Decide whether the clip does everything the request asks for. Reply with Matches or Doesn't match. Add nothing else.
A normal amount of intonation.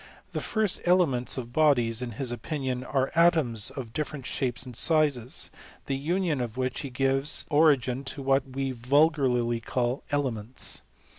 Matches